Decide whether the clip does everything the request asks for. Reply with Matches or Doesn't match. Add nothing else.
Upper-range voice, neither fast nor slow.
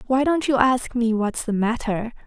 Doesn't match